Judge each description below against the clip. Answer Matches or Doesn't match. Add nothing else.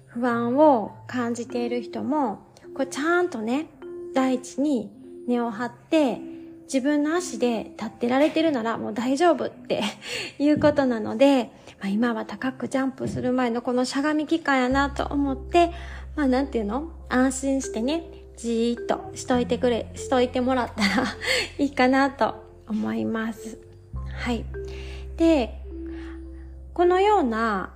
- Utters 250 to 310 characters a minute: Matches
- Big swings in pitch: Doesn't match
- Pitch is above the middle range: Matches